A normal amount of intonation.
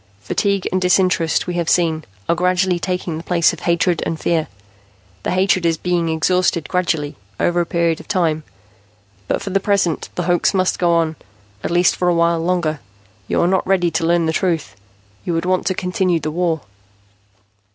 No: narrow, 1.8 semitones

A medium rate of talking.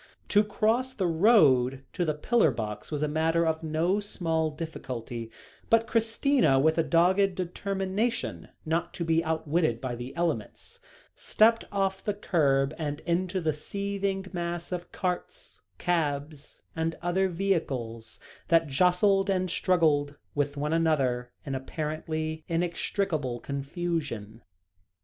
No: slow, 130 wpm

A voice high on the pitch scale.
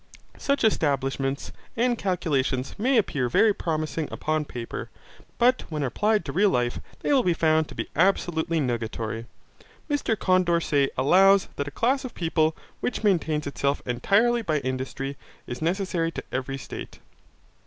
No: medium, 160 Hz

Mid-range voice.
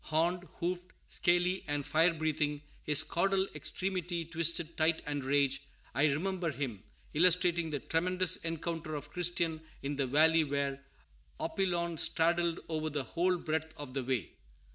Yes: medium, 160 Hz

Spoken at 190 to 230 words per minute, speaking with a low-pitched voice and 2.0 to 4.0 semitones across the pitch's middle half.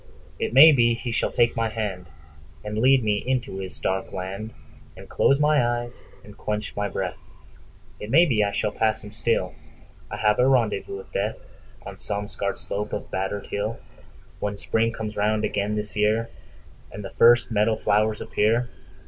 No: average, 155 wpm; low, 105 Hz; narrow, 2.4 semitones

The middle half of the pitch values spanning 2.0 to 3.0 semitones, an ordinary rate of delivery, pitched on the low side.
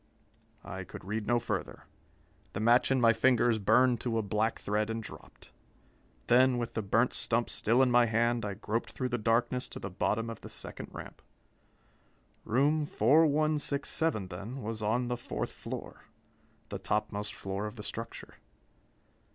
Yes: average, 2.7 semitones; average, 160 wpm; low, 115 Hz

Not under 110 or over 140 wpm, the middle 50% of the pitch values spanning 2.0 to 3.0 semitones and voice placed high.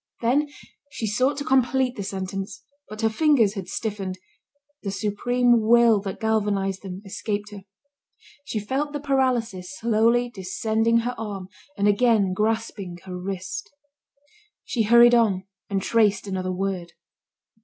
No: slow, 135 wpm; average, 3.5 semitones; high, 215 Hz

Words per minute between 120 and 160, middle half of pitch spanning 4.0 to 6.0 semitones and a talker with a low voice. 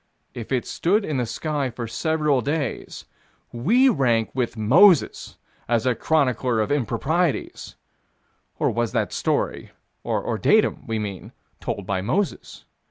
Yes: slow, 135 wpm; wide, 5.6 semitones; low, 130 Hz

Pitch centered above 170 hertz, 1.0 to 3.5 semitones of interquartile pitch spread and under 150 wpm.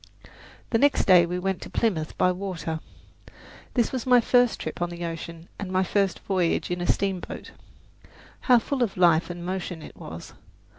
No: medium, 185 Hz; average, 3.1 semitones; average, 180 wpm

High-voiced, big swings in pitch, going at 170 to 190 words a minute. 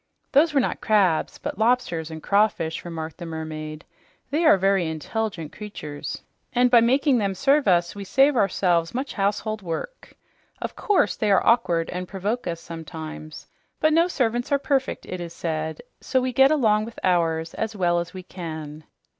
Yes: high, 195 Hz; wide, 6.7 semitones; average, 175 wpm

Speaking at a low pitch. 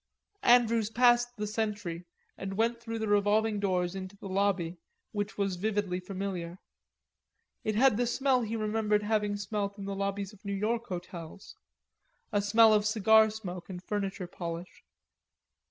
No: high, 205 Hz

